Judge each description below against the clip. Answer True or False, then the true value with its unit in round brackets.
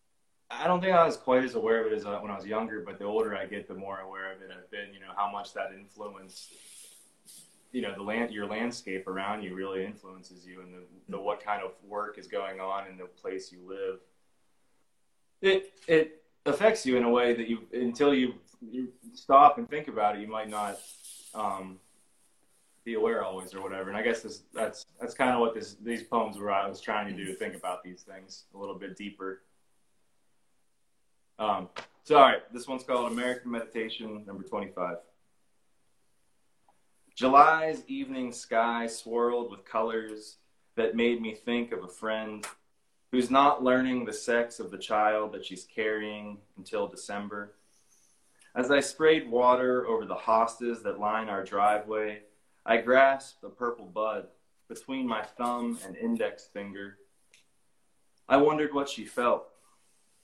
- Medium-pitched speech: False (110 Hz)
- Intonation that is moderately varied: True (3.9 semitones)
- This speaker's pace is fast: False (175 wpm)